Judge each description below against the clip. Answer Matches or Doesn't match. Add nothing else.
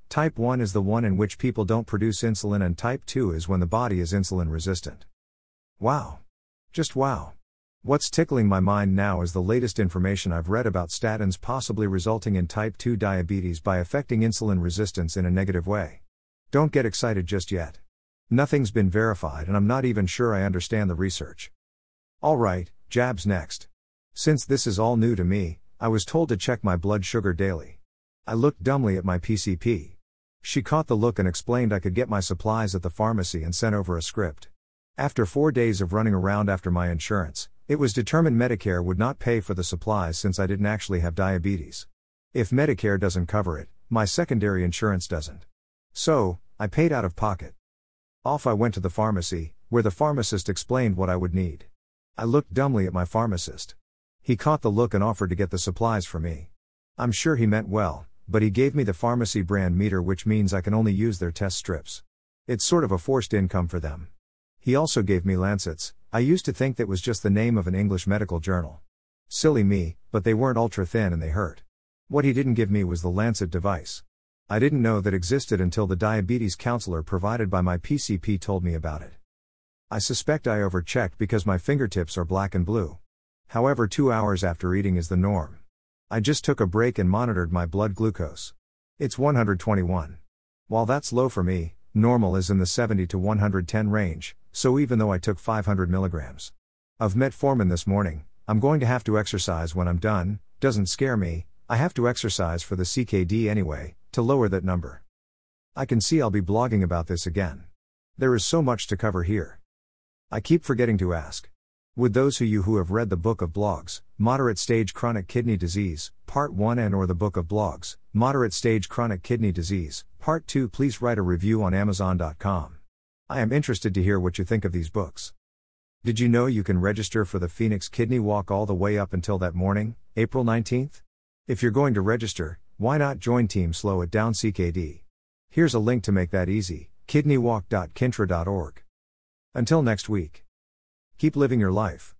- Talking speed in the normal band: Matches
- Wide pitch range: Doesn't match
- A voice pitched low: Matches